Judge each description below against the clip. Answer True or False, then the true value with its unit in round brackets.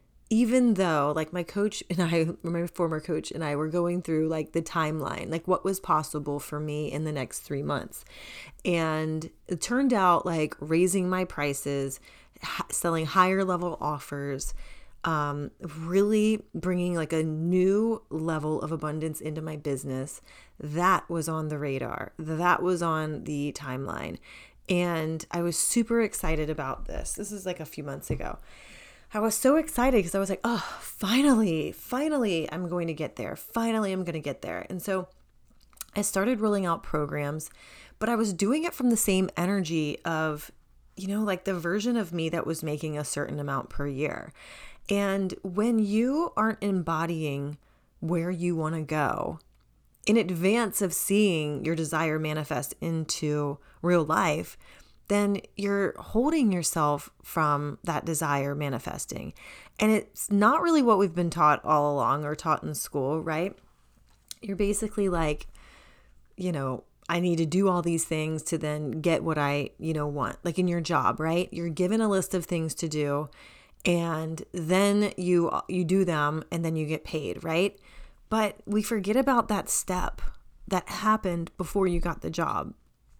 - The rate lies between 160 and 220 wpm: True (170 wpm)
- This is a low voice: False (170 Hz)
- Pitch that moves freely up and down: False (4.2 semitones)